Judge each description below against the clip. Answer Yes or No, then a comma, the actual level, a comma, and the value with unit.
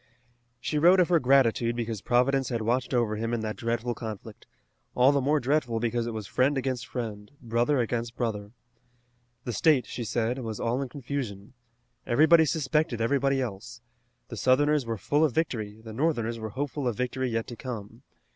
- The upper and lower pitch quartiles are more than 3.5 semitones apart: No, average, 3.2 semitones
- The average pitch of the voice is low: Yes, low, 120 Hz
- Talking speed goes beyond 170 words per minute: Yes, average, 180 wpm